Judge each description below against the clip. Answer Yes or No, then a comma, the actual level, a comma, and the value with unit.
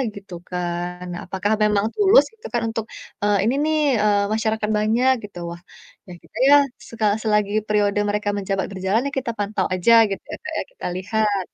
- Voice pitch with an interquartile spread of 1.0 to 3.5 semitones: Yes, narrow, 2.4 semitones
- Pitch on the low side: No, high, 210 Hz